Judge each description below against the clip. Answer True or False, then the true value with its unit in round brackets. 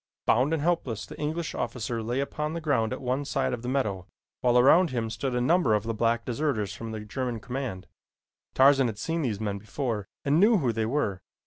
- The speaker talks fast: True (215 wpm)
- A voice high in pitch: False (125 Hz)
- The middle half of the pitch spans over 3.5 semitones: True (4.3 semitones)